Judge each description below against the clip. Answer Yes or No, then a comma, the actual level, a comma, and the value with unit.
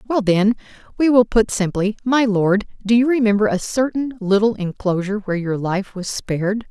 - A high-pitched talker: Yes, high, 210 Hz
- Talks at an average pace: Yes, average, 180 wpm